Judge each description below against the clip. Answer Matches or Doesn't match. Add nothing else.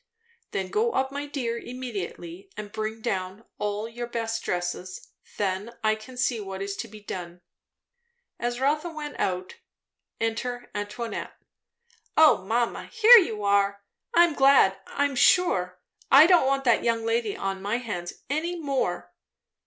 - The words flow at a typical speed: Matches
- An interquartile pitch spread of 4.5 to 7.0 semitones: Matches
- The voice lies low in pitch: Doesn't match